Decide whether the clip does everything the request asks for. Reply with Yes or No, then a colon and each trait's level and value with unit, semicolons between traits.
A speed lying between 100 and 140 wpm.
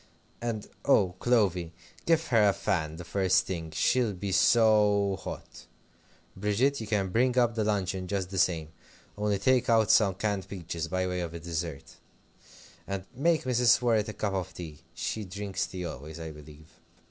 No: average, 170 wpm